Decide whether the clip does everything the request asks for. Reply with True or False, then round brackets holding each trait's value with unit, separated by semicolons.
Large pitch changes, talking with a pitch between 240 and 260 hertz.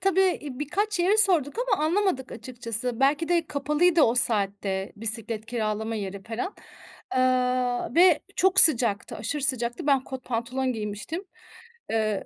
True (6.7 semitones; 255 Hz)